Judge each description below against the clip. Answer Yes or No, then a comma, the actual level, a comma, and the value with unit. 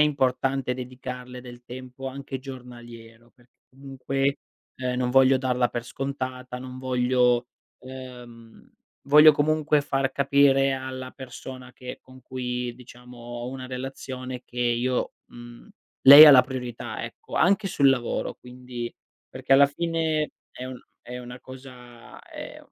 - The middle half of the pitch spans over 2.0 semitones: No, narrow, 1.5 semitones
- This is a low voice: Yes, low, 130 Hz